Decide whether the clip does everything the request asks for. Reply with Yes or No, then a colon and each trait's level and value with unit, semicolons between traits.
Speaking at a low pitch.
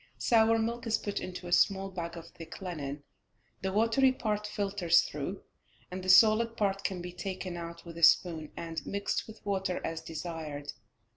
No: medium, 185 Hz